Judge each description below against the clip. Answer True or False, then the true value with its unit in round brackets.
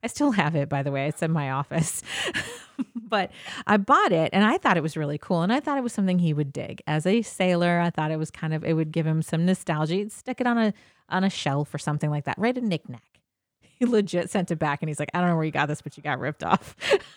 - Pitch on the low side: False (165 Hz)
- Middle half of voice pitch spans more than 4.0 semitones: True (4.9 semitones)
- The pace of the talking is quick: True (285 wpm)